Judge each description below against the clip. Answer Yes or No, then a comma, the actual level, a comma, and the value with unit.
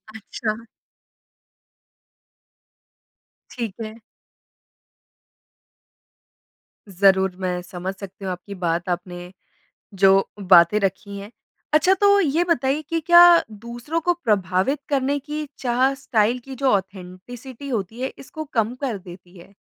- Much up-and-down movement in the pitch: Yes, wide, 6.4 semitones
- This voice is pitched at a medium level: No, high, 215 Hz